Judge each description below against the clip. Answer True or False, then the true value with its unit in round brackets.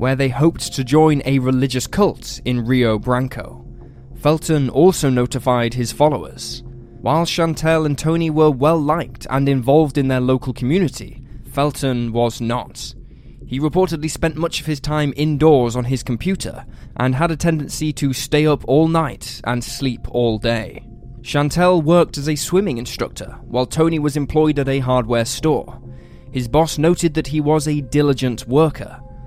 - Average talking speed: True (160 wpm)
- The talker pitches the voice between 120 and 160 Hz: True (135 Hz)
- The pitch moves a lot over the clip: False (3.8 semitones)